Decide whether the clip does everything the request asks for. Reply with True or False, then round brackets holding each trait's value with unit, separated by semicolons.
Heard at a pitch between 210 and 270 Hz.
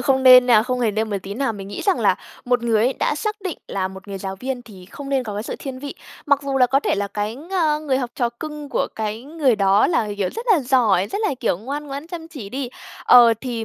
True (250 Hz)